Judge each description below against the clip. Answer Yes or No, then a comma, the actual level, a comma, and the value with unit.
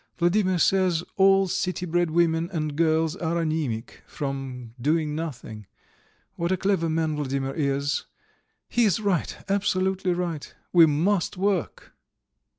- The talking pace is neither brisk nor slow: No, slow, 130 wpm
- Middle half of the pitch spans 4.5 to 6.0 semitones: No, average, 3.7 semitones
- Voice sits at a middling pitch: Yes, medium, 165 Hz